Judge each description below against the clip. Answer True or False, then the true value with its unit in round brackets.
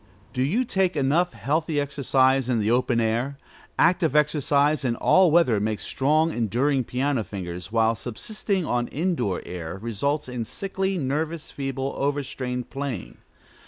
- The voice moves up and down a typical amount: True (4.7 semitones)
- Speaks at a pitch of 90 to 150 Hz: True (135 Hz)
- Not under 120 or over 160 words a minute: True (145 wpm)